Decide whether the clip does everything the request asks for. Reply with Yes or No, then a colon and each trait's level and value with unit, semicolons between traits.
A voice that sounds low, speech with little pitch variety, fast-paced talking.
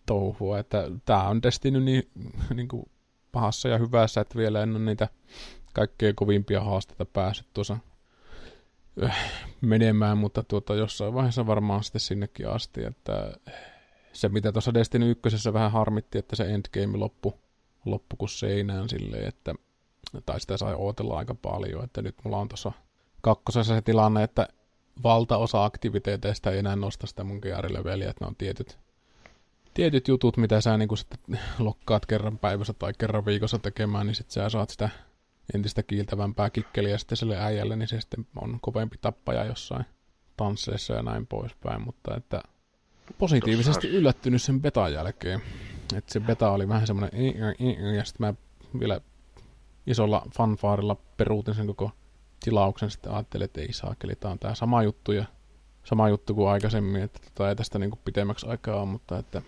Yes: low, 105 Hz; narrow, 2.1 semitones; fast, 160 wpm